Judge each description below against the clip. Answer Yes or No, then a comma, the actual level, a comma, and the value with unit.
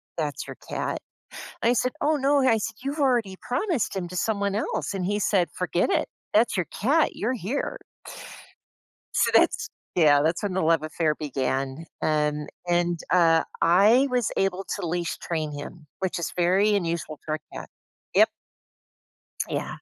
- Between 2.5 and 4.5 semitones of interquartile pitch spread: No, wide, 5.5 semitones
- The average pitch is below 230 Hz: Yes, medium, 185 Hz